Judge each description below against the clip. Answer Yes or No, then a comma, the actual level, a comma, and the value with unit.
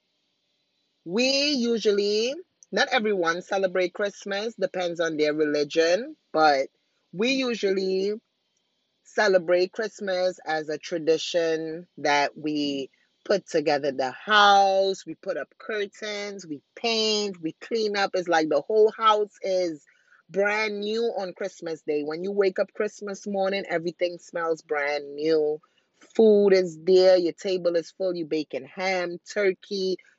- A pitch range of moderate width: Yes, average, 4.1 semitones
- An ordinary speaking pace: No, slow, 130 wpm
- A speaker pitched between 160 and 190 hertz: Yes, medium, 185 Hz